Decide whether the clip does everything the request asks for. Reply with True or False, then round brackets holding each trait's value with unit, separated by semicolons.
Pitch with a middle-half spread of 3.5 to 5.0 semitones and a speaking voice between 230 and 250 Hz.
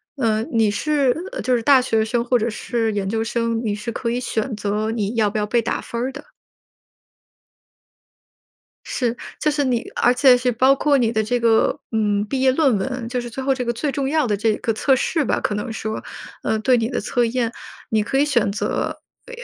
False (3.0 semitones; 235 Hz)